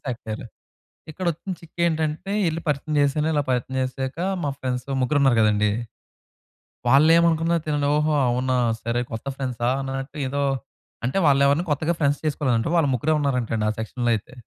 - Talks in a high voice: No, medium, 140 Hz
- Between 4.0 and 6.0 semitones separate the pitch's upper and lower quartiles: No, average, 3.6 semitones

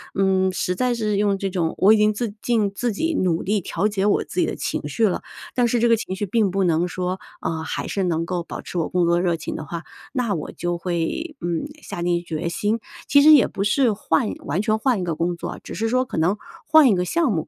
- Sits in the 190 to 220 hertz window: Yes, high, 195 Hz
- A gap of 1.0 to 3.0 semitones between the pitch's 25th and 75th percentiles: No, average, 4.5 semitones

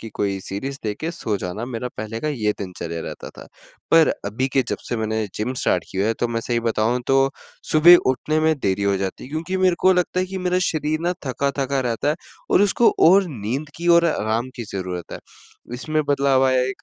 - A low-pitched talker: Yes, low, 130 Hz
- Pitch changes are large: Yes, wide, 6.3 semitones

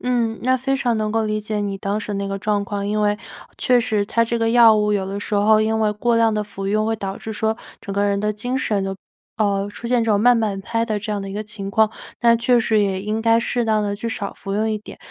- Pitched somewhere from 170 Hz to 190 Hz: No, high, 215 Hz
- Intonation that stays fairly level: Yes, narrow, 1.9 semitones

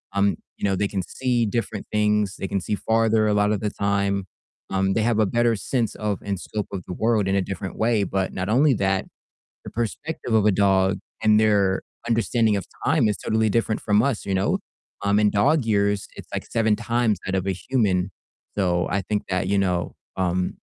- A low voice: Yes, low, 105 Hz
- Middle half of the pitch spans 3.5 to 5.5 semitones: No, narrow, 2.4 semitones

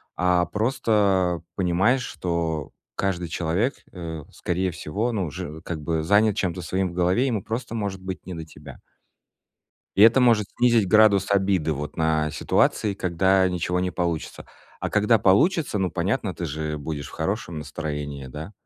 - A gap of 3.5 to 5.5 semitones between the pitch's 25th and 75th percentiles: Yes, average, 4.1 semitones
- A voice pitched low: Yes, very low, 90 Hz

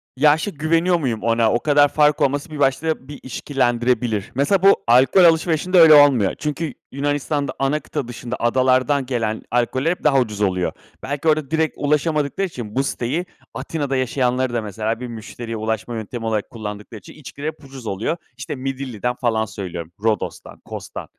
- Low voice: Yes, low, 130 Hz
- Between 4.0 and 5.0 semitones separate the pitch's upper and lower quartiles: Yes, average, 4.4 semitones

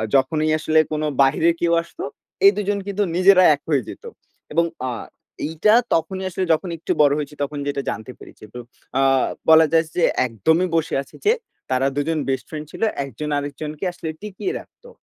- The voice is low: No, medium, 160 Hz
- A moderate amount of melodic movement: Yes, average, 3.8 semitones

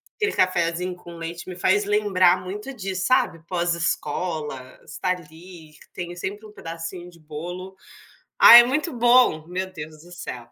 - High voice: No, medium, 180 Hz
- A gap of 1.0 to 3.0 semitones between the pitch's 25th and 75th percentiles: Yes, narrow, 2.5 semitones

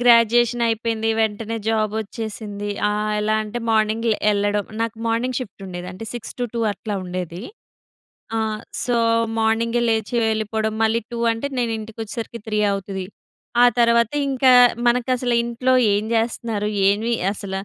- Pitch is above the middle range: Yes, high, 225 Hz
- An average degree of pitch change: No, narrow, 2.0 semitones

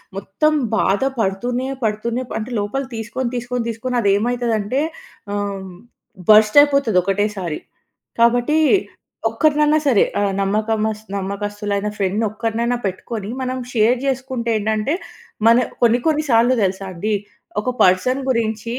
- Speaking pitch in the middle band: No, high, 225 Hz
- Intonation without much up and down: No, average, 3.3 semitones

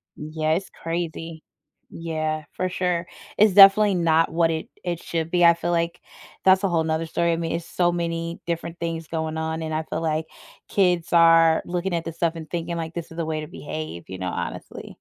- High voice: No, medium, 165 Hz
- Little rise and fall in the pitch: Yes, narrow, 1.4 semitones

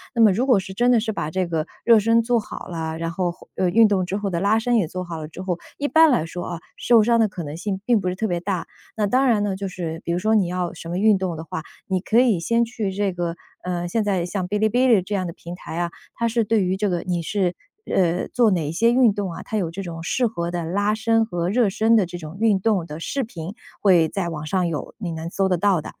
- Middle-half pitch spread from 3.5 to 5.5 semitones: Yes, average, 4.1 semitones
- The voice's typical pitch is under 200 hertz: Yes, high, 190 Hz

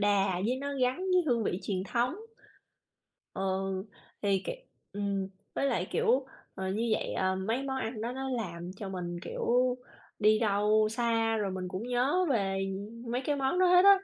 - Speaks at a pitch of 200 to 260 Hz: Yes, high, 225 Hz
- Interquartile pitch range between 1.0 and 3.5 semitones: No, average, 5.0 semitones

